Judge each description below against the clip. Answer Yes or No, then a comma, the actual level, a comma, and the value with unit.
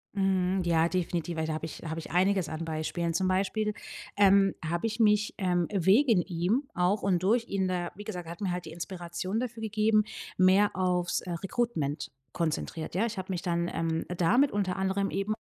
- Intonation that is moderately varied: Yes, average, 3.1 semitones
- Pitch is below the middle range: No, medium, 185 Hz